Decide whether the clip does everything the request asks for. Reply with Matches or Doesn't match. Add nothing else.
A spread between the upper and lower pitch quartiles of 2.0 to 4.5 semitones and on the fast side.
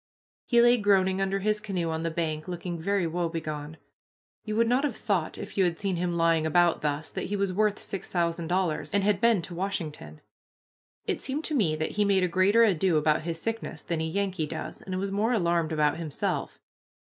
Matches